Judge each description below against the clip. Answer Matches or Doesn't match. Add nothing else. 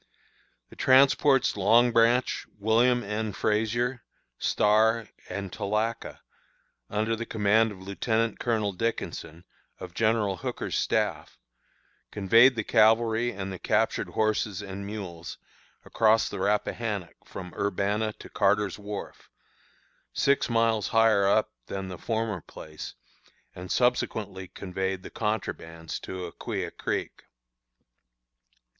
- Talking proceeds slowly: Matches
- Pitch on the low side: Matches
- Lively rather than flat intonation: Doesn't match